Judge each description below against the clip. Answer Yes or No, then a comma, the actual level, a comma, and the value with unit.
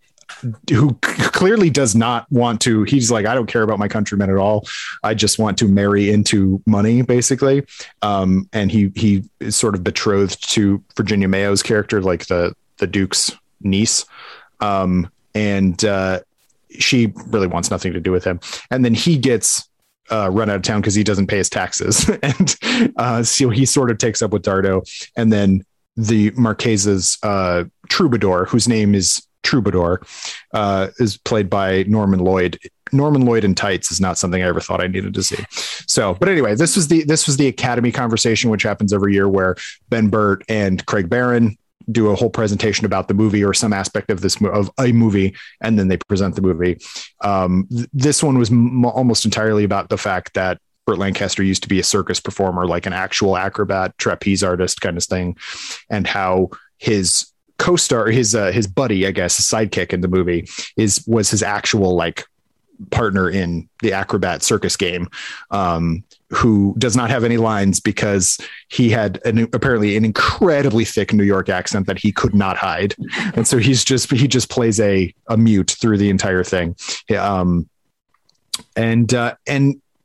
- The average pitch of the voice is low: Yes, low, 105 Hz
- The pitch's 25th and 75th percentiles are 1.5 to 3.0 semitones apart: No, average, 3.5 semitones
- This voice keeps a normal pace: Yes, average, 185 wpm